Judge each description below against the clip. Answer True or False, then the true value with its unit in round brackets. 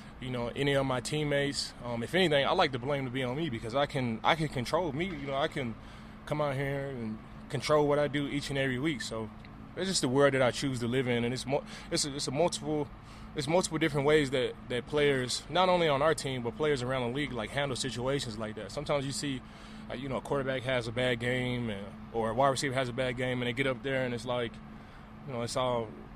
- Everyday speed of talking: False (255 wpm)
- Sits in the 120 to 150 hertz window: True (135 Hz)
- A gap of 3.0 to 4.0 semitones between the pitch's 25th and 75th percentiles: True (3.3 semitones)